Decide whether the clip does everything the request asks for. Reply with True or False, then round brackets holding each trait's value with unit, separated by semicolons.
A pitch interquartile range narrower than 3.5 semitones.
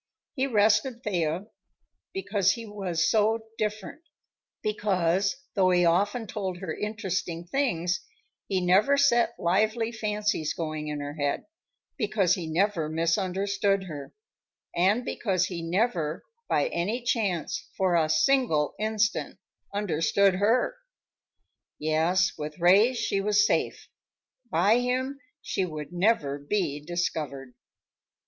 False (4.3 semitones)